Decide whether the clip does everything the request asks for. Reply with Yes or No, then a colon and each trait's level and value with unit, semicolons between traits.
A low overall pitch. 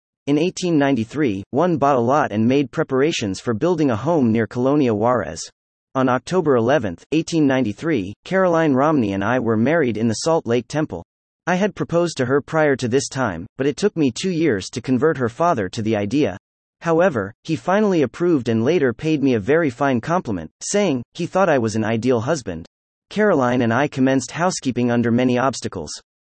Yes: low, 130 Hz